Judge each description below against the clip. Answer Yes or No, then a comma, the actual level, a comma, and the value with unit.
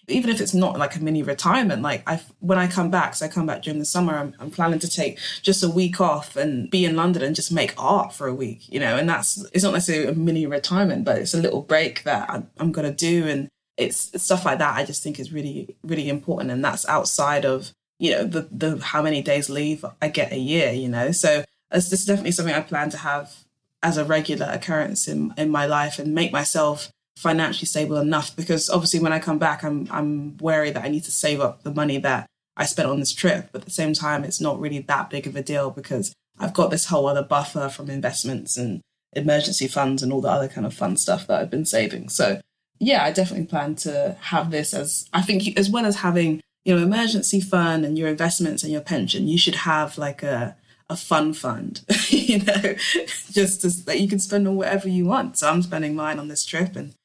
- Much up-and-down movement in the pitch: No, average, 3.7 semitones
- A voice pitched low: No, medium, 155 Hz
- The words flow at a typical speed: No, fast, 240 wpm